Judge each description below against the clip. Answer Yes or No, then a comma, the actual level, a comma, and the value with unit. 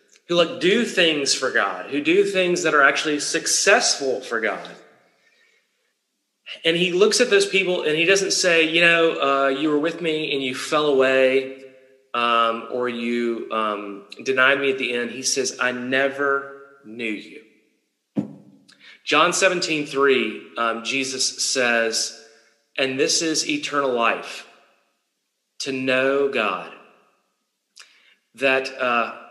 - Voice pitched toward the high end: No, medium, 140 Hz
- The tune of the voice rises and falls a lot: No, average, 4.1 semitones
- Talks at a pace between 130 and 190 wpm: Yes, slow, 135 wpm